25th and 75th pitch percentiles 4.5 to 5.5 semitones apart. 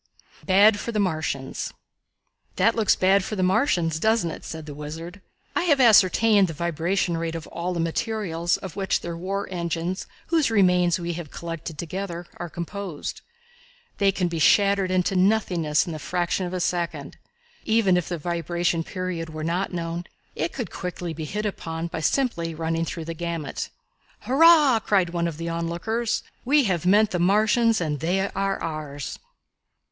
No: average, 3.2 semitones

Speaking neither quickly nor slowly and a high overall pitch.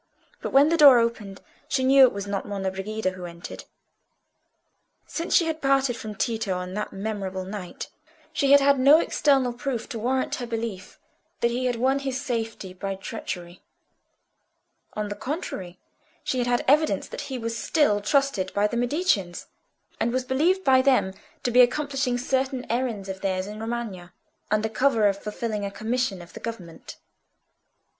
Yes: average, 170 wpm; high, 230 Hz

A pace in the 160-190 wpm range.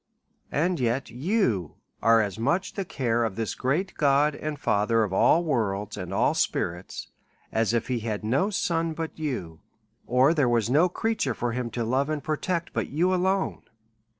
Yes: average, 180 wpm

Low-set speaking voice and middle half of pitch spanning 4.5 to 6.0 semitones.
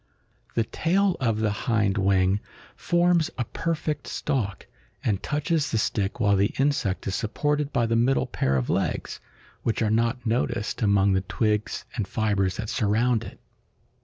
Yes: low, 110 Hz; average, 5.1 semitones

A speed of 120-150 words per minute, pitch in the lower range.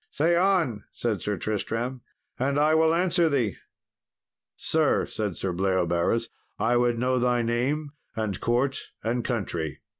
Yes: average, 140 wpm; low, 120 Hz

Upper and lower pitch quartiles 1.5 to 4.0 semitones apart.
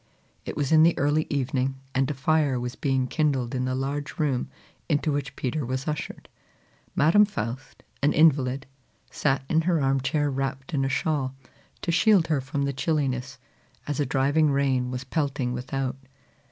Yes: narrow, 2.4 semitones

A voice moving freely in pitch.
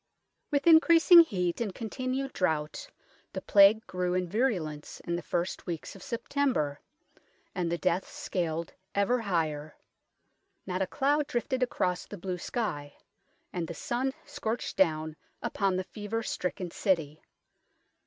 Yes: wide, 5.9 semitones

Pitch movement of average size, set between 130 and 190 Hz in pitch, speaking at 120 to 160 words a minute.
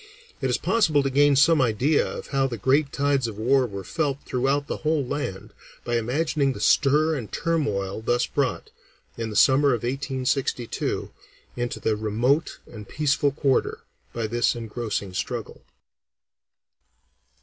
Yes: average, 3.7 semitones; low, 135 Hz; average, 150 wpm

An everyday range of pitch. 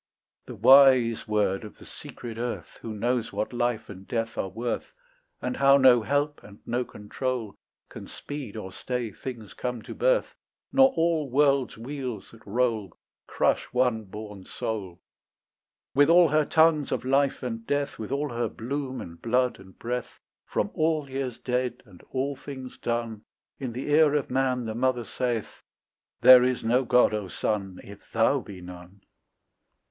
Yes: average, 3.7 semitones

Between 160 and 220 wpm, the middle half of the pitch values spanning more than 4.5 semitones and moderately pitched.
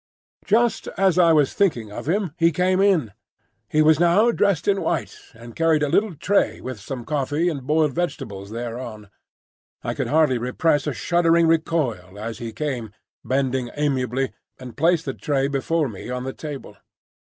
Yes: average, 170 wpm; average, 5.1 semitones; medium, 145 Hz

